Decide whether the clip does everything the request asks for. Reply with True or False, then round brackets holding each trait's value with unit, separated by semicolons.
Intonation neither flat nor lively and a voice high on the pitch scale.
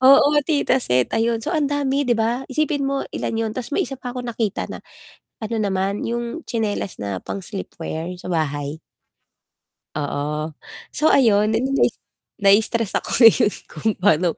False (6.3 semitones; 225 Hz)